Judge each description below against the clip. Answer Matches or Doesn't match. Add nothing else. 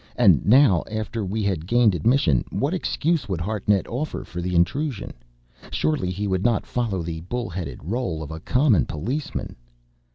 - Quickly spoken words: Doesn't match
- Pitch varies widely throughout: Matches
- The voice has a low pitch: Matches